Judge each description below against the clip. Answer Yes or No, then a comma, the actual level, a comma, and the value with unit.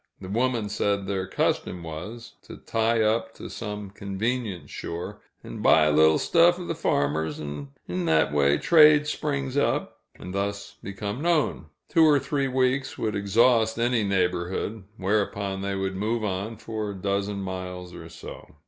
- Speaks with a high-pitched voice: No, low, 100 Hz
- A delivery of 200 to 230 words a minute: No, average, 165 wpm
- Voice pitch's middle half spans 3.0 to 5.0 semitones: Yes, average, 4.2 semitones